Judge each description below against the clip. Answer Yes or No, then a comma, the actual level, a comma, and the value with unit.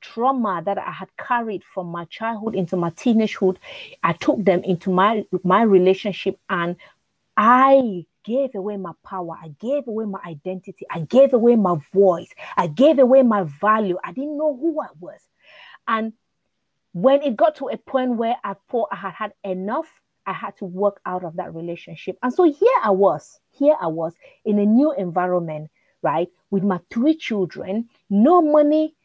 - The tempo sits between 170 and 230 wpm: Yes, average, 180 wpm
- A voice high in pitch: Yes, high, 205 Hz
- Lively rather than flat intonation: Yes, wide, 5.9 semitones